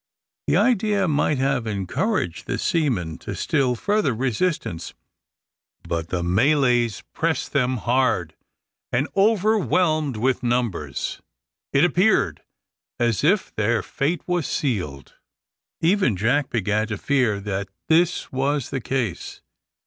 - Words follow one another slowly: Yes, slow, 120 wpm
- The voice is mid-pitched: No, low, 130 Hz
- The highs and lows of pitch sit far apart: Yes, wide, 7.0 semitones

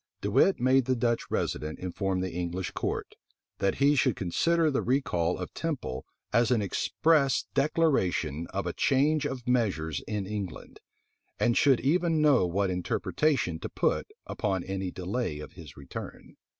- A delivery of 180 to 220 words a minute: No, average, 155 wpm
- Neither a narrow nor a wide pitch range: No, wide, 7.4 semitones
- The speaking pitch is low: Yes, low, 105 Hz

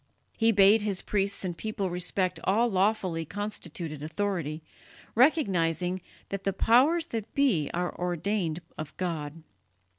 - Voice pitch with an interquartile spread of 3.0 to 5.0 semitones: Yes, average, 4.0 semitones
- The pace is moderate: No, slow, 125 wpm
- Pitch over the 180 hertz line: Yes, high, 190 Hz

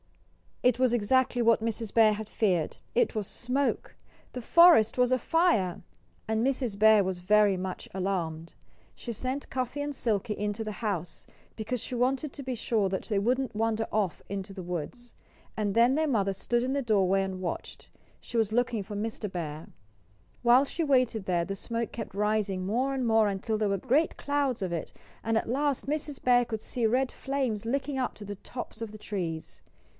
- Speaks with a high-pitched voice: Yes, high, 225 Hz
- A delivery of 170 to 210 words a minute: Yes, average, 190 wpm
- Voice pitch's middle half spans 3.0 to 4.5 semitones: Yes, average, 4.2 semitones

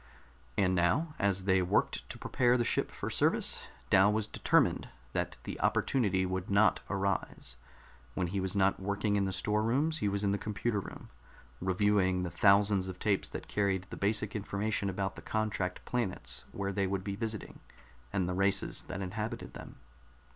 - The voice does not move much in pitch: Yes, narrow, 2.1 semitones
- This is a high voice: No, low, 100 Hz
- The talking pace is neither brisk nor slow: Yes, average, 175 wpm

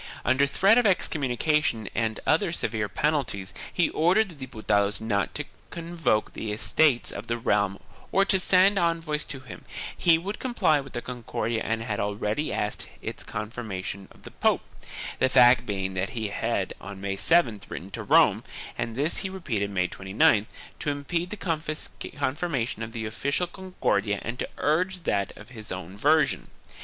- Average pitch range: No, wide, 7.8 semitones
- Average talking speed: Yes, average, 175 wpm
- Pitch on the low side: Yes, low, 125 Hz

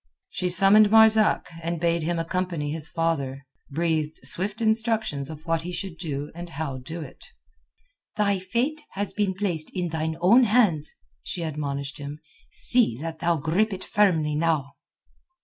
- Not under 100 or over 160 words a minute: Yes, average, 155 wpm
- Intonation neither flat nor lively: Yes, average, 4.4 semitones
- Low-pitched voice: No, medium, 170 Hz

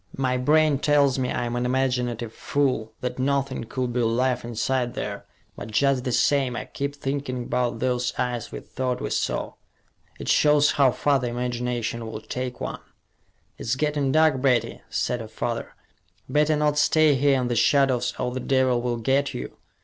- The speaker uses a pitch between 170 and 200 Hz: No, low, 125 Hz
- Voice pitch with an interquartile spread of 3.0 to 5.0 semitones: No, narrow, 2.4 semitones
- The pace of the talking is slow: No, average, 175 wpm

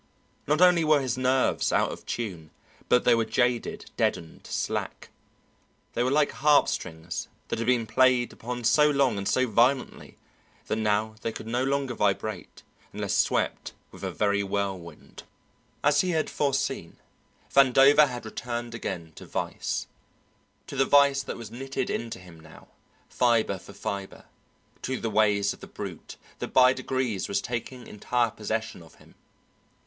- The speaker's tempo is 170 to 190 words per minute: No, average, 155 wpm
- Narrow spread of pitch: No, average, 4.1 semitones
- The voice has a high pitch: No, low, 120 Hz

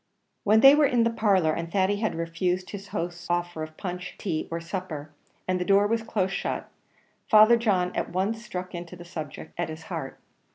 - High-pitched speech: No, medium, 180 Hz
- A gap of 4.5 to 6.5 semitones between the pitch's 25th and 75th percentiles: No, average, 3.4 semitones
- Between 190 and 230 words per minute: Yes, average, 200 wpm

